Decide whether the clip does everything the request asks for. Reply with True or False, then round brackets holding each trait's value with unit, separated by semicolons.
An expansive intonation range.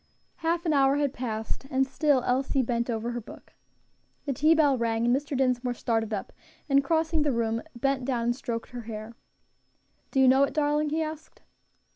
False (3.6 semitones)